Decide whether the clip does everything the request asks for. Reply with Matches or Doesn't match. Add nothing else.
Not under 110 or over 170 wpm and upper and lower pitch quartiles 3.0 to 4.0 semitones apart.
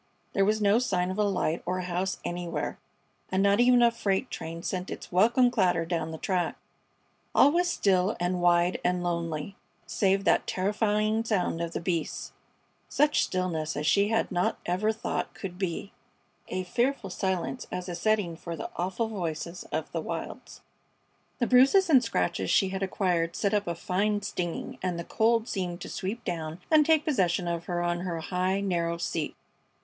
Doesn't match